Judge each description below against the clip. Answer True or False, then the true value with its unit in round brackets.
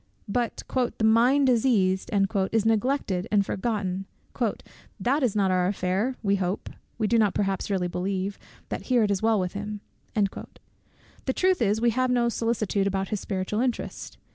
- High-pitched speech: True (210 Hz)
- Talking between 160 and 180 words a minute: True (165 wpm)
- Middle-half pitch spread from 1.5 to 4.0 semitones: True (3.4 semitones)